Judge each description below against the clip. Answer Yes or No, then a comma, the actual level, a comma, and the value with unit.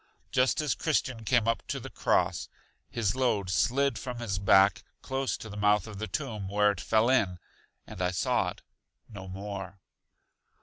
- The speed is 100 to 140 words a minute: No, average, 175 wpm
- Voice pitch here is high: No, low, 105 Hz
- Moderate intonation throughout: Yes, average, 4.2 semitones